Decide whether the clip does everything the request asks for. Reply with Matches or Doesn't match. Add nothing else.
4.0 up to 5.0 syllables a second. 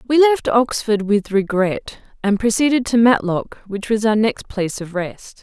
Matches